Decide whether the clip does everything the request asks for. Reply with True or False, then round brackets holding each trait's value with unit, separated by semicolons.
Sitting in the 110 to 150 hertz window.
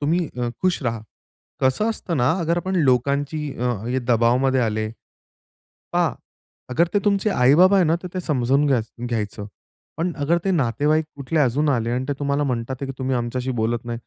True (135 Hz)